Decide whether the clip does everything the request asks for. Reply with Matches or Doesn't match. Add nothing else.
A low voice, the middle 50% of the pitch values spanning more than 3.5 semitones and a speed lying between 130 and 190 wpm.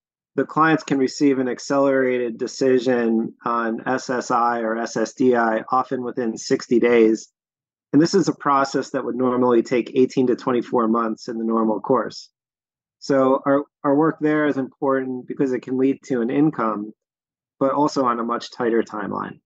Doesn't match